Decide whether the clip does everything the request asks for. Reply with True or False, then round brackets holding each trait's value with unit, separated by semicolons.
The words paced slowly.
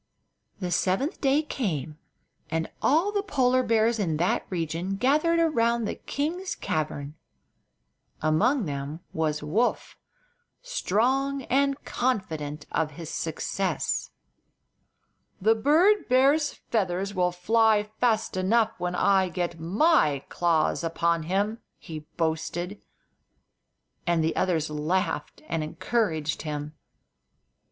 True (110 wpm)